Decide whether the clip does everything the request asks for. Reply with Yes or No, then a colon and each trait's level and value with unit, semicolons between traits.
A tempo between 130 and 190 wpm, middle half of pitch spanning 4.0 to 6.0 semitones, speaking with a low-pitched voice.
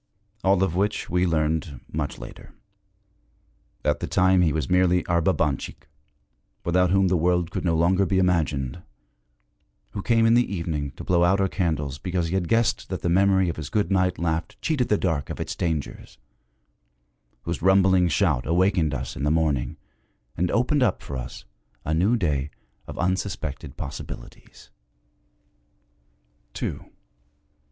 No: average, 155 wpm; average, 3.3 semitones; very low, 90 Hz